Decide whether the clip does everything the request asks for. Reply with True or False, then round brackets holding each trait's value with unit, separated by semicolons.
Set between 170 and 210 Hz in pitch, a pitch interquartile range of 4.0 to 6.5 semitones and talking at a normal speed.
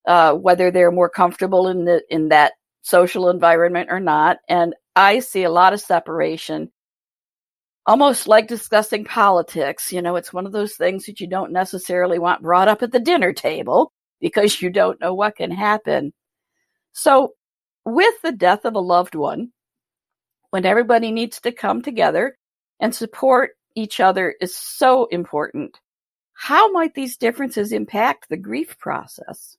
True (190 Hz; 5.1 semitones; 160 wpm)